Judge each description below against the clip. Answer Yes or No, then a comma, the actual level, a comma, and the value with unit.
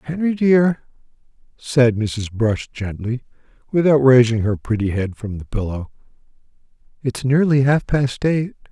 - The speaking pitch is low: Yes, low, 125 Hz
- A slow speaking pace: Yes, slow, 130 wpm